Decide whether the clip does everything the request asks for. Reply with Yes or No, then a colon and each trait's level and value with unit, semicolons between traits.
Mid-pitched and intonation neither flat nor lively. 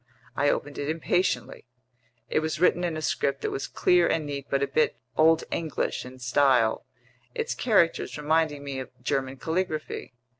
Yes: medium, 150 Hz; average, 3.0 semitones